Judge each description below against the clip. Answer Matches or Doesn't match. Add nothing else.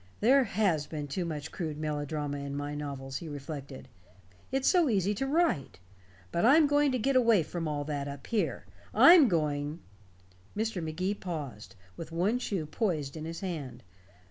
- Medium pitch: Matches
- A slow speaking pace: Doesn't match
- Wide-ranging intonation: Matches